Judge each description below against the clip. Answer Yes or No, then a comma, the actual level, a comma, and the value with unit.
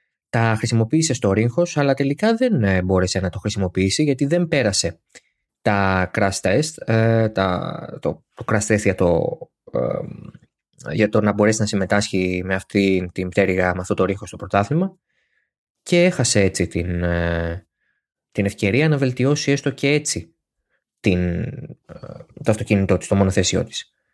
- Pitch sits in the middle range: No, low, 100 Hz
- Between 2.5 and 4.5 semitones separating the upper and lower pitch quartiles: No, average, 5.1 semitones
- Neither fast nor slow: Yes, average, 140 wpm